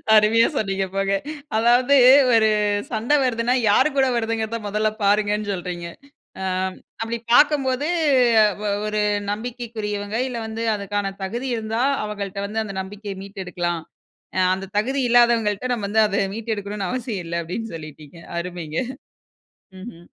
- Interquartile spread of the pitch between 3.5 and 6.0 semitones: No, average, 3.0 semitones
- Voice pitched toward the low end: No, high, 210 Hz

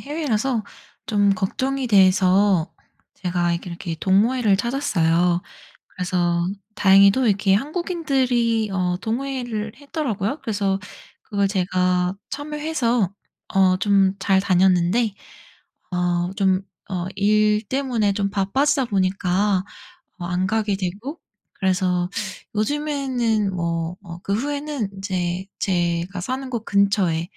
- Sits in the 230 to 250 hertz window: No, high, 200 Hz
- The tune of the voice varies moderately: Yes, average, 4.6 semitones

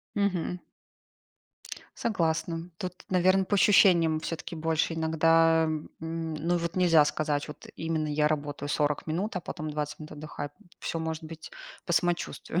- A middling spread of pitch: No, narrow, 2.1 semitones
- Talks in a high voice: No, medium, 165 Hz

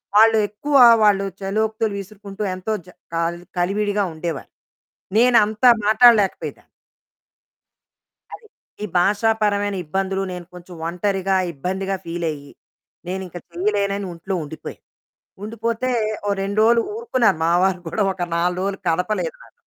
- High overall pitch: Yes, high, 200 Hz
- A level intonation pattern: No, average, 3.1 semitones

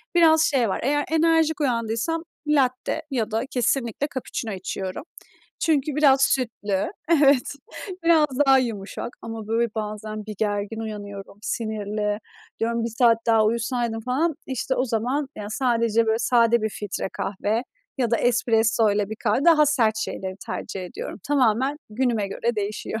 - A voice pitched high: Yes, high, 230 Hz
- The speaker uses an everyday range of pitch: Yes, average, 3.7 semitones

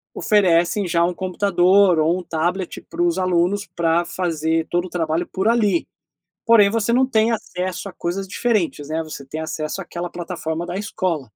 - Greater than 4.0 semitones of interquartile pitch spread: No, average, 3.1 semitones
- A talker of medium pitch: Yes, medium, 180 Hz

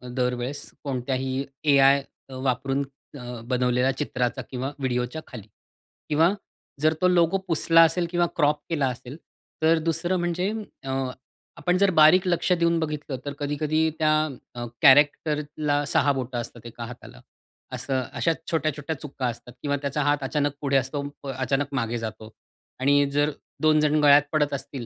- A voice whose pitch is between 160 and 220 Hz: No, medium, 145 Hz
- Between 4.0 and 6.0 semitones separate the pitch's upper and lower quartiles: No, average, 3.2 semitones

